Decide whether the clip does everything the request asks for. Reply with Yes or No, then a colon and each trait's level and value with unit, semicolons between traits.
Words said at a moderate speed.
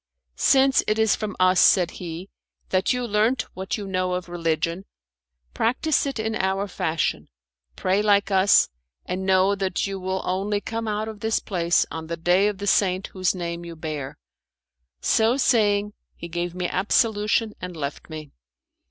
Yes: average, 170 wpm